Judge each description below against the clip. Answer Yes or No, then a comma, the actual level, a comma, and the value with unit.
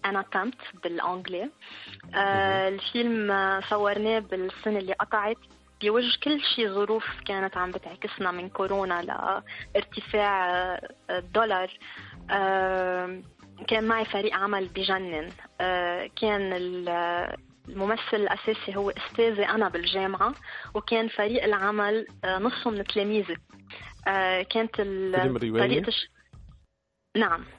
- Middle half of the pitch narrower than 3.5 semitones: Yes, average, 2.7 semitones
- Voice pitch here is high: Yes, high, 195 Hz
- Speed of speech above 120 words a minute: No, average, 95 wpm